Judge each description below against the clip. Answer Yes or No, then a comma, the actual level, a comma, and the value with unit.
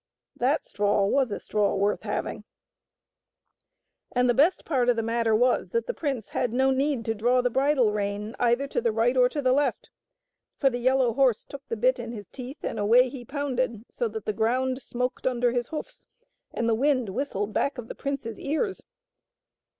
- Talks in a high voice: Yes, high, 245 Hz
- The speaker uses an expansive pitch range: No, average, 3.2 semitones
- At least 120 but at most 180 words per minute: No, average, 200 wpm